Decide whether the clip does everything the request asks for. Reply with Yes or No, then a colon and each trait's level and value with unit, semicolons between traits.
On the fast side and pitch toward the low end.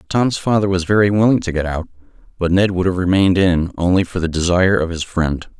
Yes: fast, 225 wpm; very low, 90 Hz